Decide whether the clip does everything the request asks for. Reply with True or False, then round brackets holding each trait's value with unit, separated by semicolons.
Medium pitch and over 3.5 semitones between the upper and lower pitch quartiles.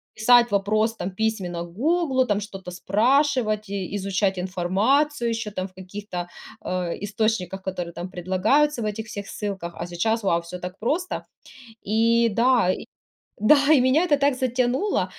False (210 Hz; 4.9 semitones)